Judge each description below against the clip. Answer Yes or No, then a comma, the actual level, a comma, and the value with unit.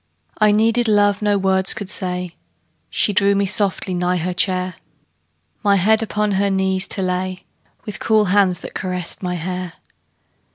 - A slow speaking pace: No, average, 160 wpm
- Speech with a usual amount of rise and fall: No, narrow, 2.1 semitones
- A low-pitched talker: No, high, 190 Hz